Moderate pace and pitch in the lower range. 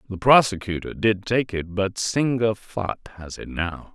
Yes: average, 165 wpm; low, 105 Hz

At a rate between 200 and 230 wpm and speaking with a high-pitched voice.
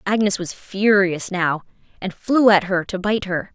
No: average, 185 wpm; high, 195 Hz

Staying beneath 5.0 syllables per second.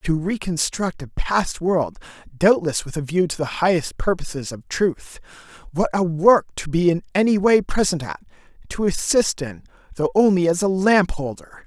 Yes: 4.6 syllables/s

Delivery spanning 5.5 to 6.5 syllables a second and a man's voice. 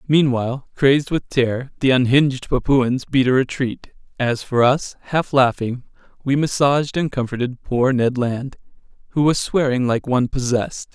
No: 5.0 syllables/s; male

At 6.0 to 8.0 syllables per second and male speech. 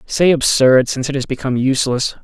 Yes: 6.3 syllables/s; male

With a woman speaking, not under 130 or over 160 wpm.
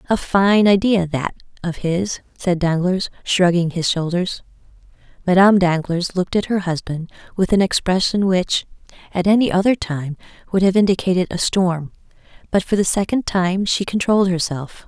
Yes: female; average, 155 wpm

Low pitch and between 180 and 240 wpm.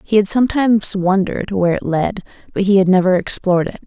No: high, 195 Hz; average, 200 wpm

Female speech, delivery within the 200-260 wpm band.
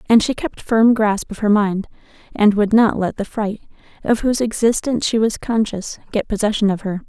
Yes: female; fast, 205 wpm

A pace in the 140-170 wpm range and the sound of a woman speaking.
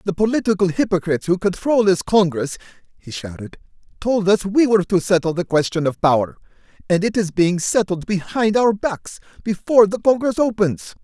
No: average, 165 wpm; male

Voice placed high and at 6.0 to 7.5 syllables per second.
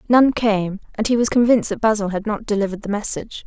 Yes: high, 215 Hz; 6.6 syllables/s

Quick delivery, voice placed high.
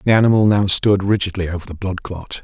No: fast, 220 wpm; very low, 95 Hz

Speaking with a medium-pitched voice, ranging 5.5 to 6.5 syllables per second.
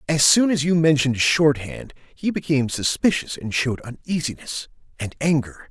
No: medium, 145 Hz; 5.1 syllables/s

